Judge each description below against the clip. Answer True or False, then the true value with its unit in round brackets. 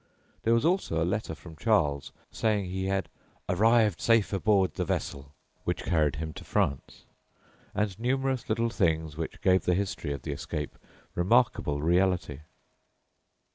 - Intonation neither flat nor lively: False (5.7 semitones)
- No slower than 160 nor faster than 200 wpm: False (145 wpm)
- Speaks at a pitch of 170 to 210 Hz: False (95 Hz)